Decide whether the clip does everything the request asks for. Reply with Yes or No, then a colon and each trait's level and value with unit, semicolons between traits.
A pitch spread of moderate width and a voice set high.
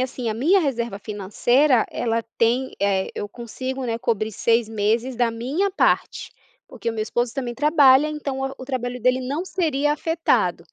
Yes: average, 3.4 semitones; very high, 250 Hz